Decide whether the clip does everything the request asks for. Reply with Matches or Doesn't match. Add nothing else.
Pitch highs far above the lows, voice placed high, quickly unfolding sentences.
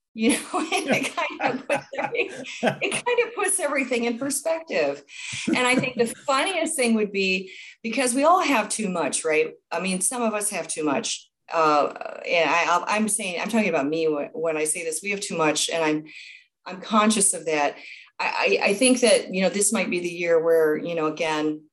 Matches